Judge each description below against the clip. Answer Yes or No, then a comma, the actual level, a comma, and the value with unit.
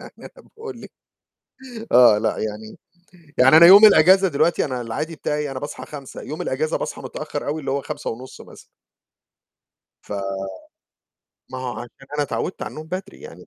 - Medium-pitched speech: Yes, medium, 145 Hz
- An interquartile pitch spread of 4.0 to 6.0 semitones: Yes, average, 4.3 semitones